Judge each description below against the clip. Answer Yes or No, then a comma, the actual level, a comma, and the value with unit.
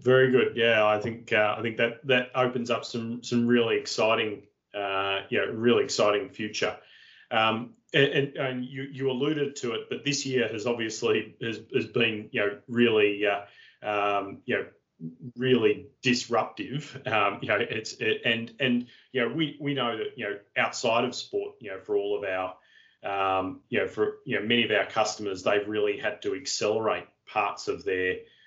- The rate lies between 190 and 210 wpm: Yes, average, 195 wpm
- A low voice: Yes, low, 125 Hz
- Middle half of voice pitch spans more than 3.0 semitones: Yes, average, 4.4 semitones